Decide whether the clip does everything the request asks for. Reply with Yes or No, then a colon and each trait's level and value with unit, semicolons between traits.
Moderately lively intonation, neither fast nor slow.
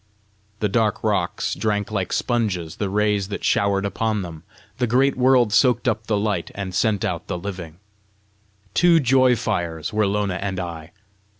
Yes: average, 3.3 semitones; average, 165 wpm